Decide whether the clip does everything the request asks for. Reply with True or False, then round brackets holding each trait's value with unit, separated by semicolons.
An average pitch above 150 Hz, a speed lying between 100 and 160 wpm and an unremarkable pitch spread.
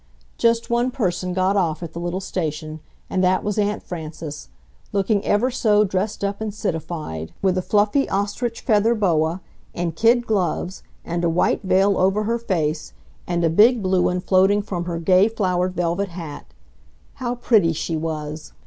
False (185 Hz; 170 wpm; 3.7 semitones)